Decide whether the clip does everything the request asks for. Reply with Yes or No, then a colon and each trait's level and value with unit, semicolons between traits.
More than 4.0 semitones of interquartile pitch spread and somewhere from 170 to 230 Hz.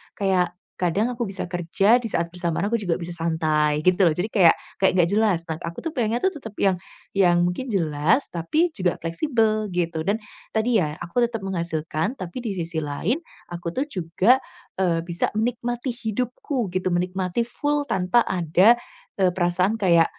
Yes: average, 5.1 semitones; medium, 185 Hz